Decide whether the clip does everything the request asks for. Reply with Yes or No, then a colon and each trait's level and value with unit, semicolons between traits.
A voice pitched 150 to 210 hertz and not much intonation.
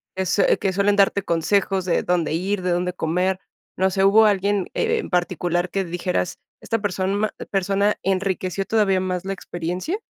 Yes: high, 190 Hz; narrow, 1.8 semitones